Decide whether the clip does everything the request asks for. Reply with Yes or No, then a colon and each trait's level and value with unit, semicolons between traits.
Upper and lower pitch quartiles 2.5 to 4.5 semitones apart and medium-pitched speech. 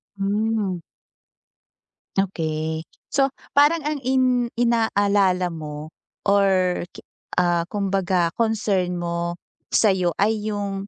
No: average, 3.9 semitones; high, 195 Hz